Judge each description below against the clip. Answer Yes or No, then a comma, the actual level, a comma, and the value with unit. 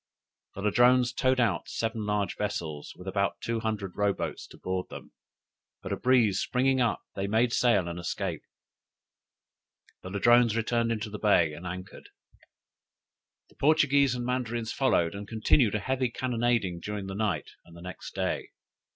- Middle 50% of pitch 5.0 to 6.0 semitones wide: No, average, 4.1 semitones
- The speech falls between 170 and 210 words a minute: No, average, 160 wpm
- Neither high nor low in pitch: No, low, 110 Hz